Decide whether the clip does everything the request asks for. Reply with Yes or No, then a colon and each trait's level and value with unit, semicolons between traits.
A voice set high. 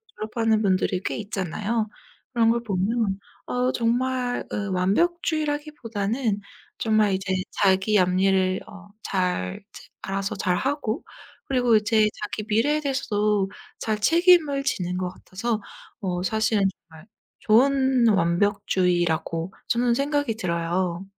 Yes: high, 210 Hz